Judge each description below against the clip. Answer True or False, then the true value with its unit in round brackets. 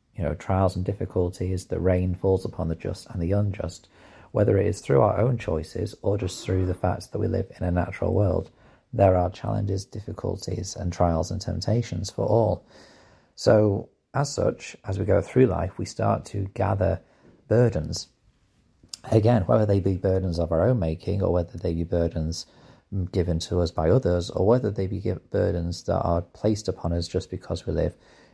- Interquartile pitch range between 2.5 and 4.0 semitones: True (3.2 semitones)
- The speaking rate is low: False (190 wpm)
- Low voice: True (95 Hz)